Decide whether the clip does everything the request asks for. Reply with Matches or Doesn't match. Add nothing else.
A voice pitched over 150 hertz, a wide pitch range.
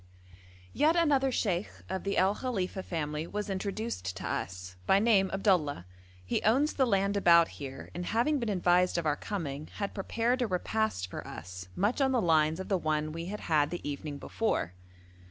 Matches